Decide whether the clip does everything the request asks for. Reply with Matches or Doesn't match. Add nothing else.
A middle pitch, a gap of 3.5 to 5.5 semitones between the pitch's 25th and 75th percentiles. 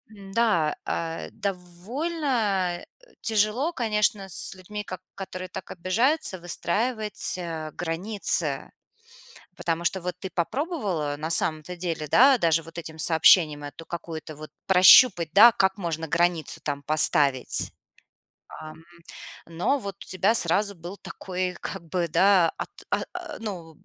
Matches